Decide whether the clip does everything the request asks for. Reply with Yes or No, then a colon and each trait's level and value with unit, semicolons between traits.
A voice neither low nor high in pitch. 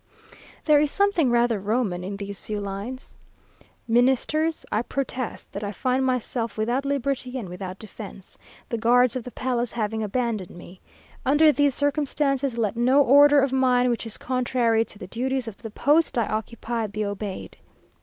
No: high, 240 Hz